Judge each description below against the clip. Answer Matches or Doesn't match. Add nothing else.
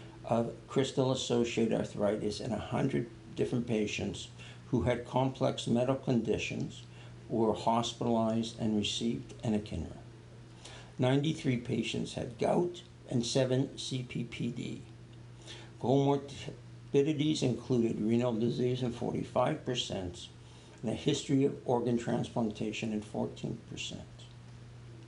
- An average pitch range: Doesn't match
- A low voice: Matches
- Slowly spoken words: Matches